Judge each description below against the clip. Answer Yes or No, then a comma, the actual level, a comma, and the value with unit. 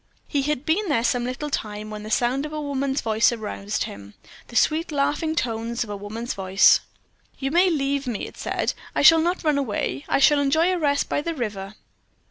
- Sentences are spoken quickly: Yes, fast, 210 wpm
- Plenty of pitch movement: Yes, wide, 5.7 semitones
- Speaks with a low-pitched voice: No, very high, 270 Hz